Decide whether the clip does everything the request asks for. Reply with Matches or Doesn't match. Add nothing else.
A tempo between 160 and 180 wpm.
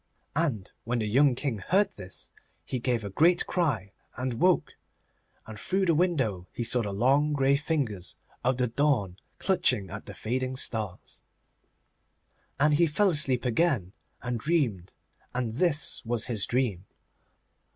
Doesn't match